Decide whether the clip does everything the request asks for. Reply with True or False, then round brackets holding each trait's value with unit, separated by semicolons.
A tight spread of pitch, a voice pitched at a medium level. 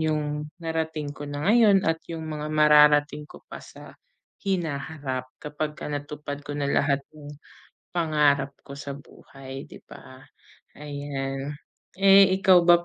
True (2.0 semitones; 150 Hz)